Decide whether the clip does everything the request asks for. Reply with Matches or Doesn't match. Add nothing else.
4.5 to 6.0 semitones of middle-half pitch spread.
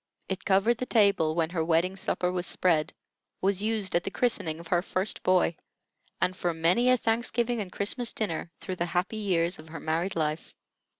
Doesn't match